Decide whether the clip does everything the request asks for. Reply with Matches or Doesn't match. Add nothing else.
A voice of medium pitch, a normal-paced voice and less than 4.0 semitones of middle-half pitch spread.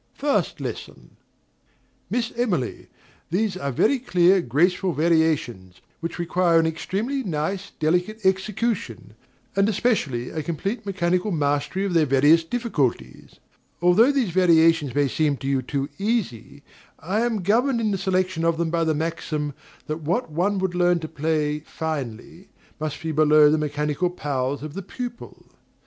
Doesn't match